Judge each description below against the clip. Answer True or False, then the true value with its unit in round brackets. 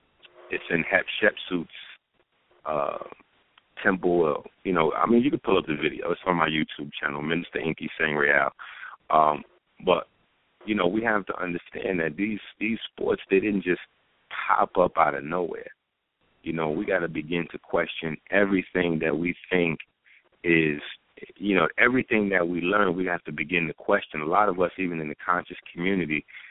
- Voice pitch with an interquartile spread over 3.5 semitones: False (3.2 semitones)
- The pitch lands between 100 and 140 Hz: False (85 Hz)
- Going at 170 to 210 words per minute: True (175 wpm)